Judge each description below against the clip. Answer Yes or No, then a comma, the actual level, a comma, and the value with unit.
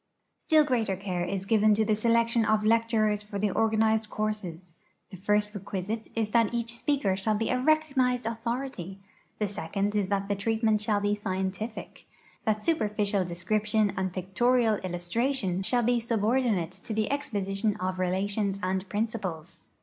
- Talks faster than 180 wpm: No, average, 160 wpm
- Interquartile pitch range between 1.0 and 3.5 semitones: Yes, average, 2.9 semitones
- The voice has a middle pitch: No, high, 210 Hz